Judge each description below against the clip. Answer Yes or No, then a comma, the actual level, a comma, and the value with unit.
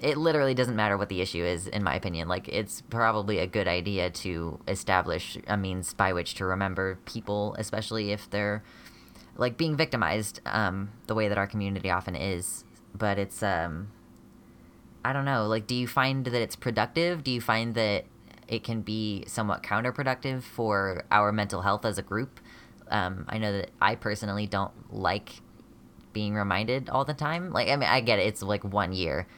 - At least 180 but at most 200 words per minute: Yes, average, 190 wpm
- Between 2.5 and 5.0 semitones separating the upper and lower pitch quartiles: Yes, average, 3.0 semitones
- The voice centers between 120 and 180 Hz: No, low, 105 Hz